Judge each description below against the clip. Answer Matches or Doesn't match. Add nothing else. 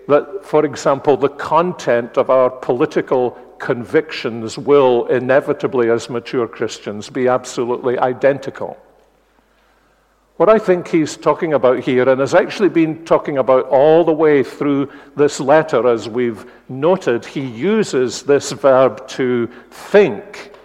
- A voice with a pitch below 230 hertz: Matches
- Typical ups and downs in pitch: Matches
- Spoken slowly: Matches